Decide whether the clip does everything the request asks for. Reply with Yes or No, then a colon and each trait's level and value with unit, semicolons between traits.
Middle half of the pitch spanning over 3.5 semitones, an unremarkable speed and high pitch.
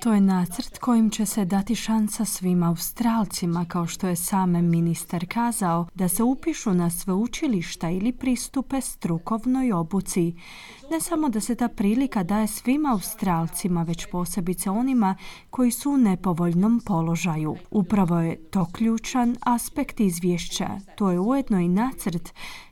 Yes: average, 5.1 semitones; average, 145 wpm; high, 200 Hz